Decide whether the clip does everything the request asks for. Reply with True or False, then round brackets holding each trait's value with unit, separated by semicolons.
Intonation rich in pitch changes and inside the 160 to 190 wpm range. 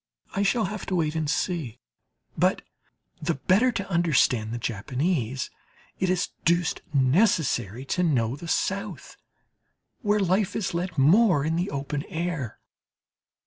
False (5.7 semitones; 140 wpm)